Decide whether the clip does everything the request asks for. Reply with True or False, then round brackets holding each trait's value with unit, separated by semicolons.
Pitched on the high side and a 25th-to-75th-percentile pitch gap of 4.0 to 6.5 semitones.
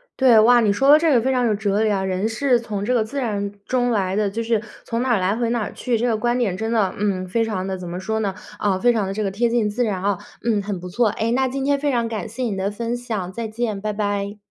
False (220 Hz; 3.1 semitones)